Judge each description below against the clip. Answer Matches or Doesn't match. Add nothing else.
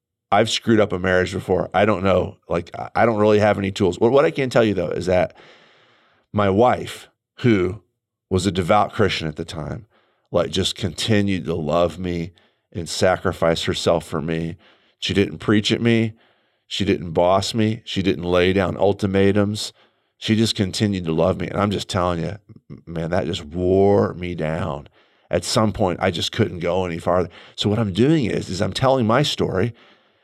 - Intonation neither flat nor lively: Matches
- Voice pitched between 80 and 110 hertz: Matches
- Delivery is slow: Doesn't match